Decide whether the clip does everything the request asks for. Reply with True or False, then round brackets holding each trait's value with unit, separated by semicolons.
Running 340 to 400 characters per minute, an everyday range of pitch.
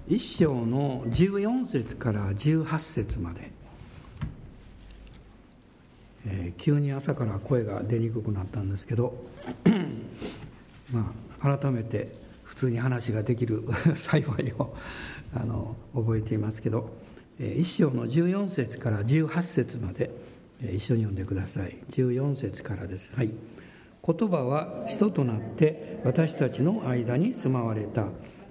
False (220 characters per minute; 4.3 semitones)